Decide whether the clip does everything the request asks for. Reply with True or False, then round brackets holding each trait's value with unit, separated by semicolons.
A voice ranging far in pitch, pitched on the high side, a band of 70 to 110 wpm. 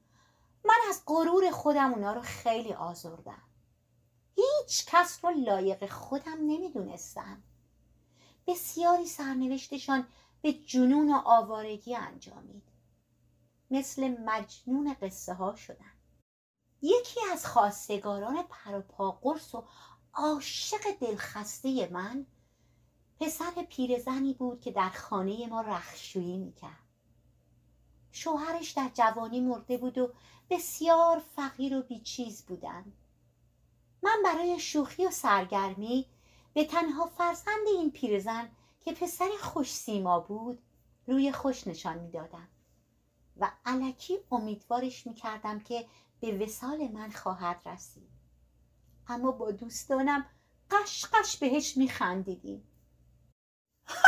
True (7.2 semitones; 250 Hz; 105 wpm)